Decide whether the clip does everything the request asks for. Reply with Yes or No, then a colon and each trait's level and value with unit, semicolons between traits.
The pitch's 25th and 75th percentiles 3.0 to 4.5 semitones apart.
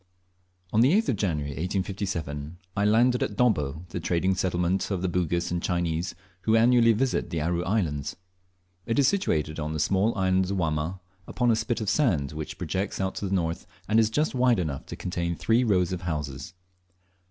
No: average, 5.1 semitones